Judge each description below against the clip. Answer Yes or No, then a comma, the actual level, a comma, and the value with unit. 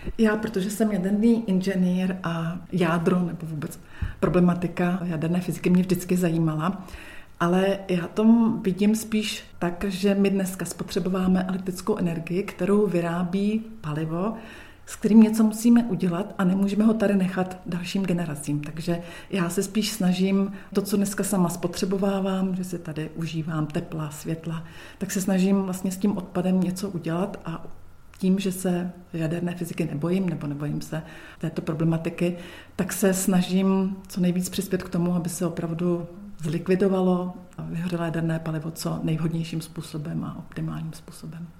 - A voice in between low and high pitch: Yes, medium, 180 Hz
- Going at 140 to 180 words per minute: Yes, average, 145 wpm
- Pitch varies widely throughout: No, narrow, 2.6 semitones